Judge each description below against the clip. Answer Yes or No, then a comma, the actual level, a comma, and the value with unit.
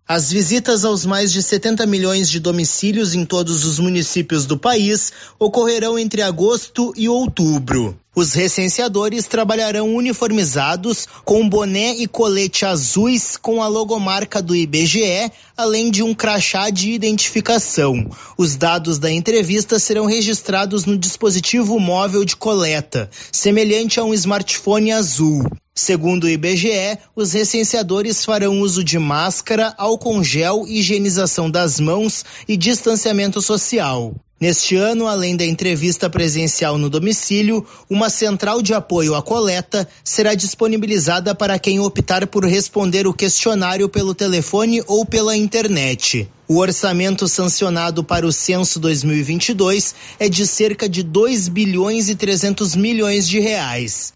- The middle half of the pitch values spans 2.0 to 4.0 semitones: Yes, average, 3.7 semitones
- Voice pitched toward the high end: Yes, high, 200 Hz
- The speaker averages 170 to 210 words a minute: No, average, 130 wpm